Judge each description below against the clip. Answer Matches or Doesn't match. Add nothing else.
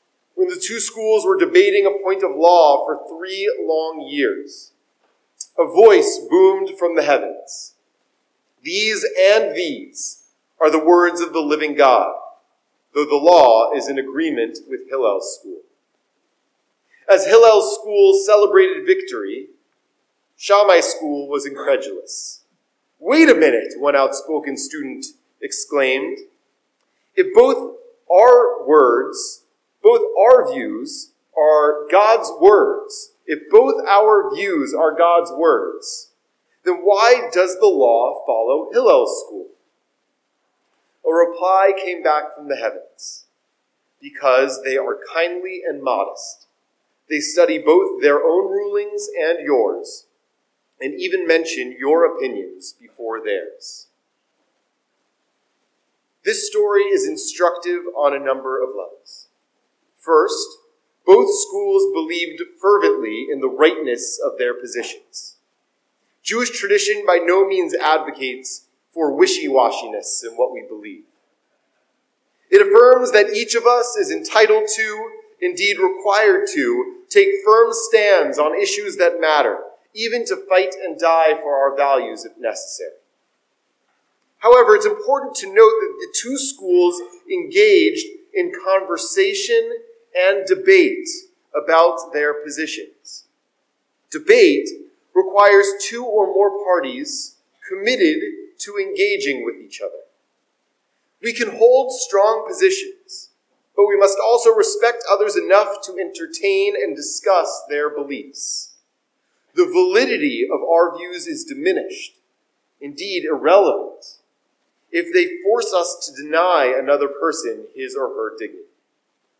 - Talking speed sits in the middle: Doesn't match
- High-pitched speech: Matches